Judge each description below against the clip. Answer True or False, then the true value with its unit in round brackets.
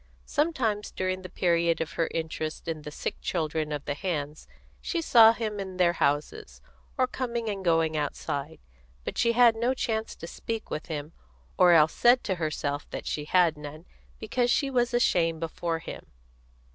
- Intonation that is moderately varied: False (6.4 semitones)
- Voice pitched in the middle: True (175 Hz)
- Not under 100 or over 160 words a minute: False (175 wpm)